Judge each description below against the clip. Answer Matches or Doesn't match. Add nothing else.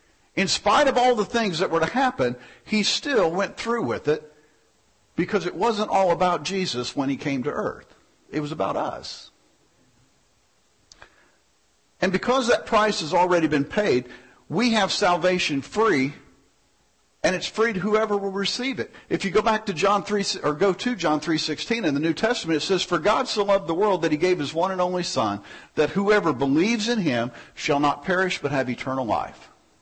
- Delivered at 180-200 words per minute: Matches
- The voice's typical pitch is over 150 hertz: Matches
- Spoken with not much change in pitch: Doesn't match